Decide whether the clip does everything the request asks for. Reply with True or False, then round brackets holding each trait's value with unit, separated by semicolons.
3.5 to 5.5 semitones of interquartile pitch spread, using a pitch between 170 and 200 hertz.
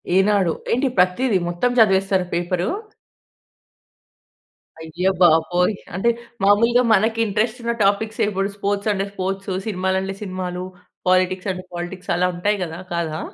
False (2.4 semitones; 190 Hz)